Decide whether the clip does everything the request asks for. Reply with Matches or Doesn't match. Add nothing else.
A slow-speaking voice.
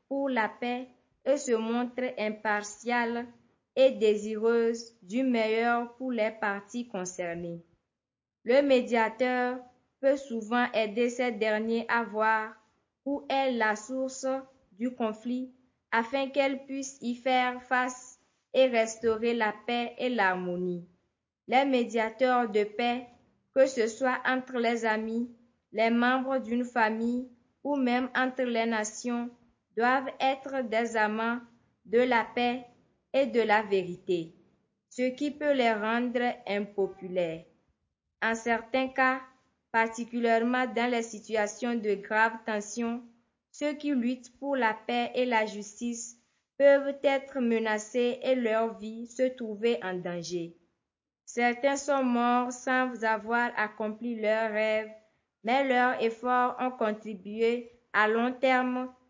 Matches